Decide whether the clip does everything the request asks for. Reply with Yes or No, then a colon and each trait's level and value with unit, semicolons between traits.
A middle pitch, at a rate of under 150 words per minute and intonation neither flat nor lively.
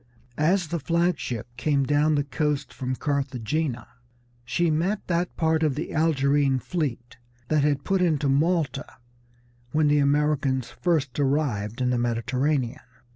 Yes: medium, 145 Hz; average, 140 wpm; average, 3.3 semitones